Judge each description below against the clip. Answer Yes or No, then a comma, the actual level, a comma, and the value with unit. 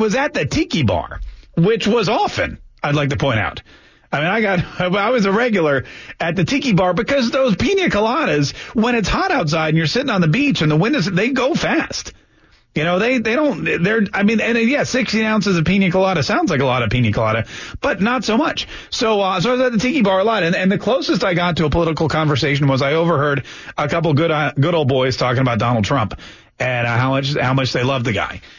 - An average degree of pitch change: No, wide, 8.6 semitones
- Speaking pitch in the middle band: Yes, medium, 165 Hz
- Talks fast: Yes, fast, 250 wpm